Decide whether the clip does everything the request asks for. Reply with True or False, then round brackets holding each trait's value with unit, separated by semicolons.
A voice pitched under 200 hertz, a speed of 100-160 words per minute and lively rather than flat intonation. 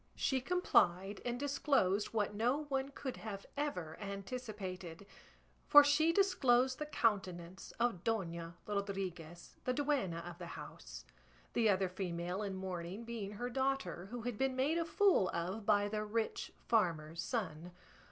False (210 Hz; 145 wpm; 6.0 semitones)